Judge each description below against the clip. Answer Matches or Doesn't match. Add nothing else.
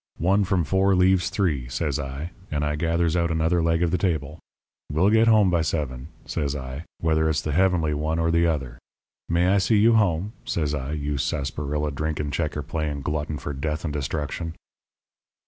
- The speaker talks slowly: Doesn't match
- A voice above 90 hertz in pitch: Doesn't match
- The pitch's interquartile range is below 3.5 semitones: Matches